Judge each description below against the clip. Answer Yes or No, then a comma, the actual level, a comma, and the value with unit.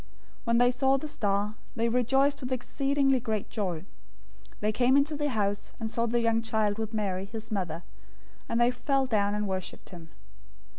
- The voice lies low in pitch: No, high, 230 Hz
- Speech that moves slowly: No, average, 190 wpm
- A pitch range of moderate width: Yes, average, 3.8 semitones